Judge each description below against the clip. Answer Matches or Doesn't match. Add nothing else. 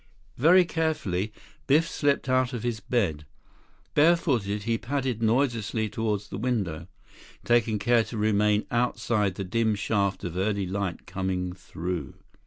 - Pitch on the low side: Matches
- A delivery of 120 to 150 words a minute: Matches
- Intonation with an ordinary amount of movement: Matches